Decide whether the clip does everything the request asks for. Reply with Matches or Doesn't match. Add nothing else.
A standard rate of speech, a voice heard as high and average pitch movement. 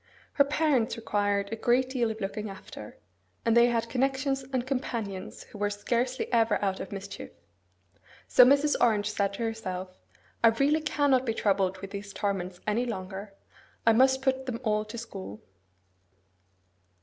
Matches